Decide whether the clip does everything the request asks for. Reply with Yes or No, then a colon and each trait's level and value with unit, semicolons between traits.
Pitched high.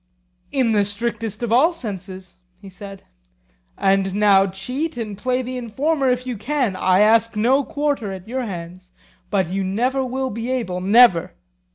Yes: high, 220 Hz